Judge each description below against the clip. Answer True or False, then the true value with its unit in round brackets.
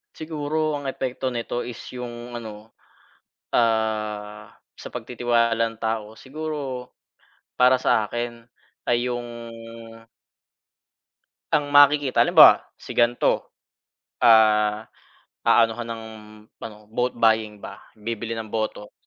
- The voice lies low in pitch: True (115 Hz)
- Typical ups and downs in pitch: False (2.3 semitones)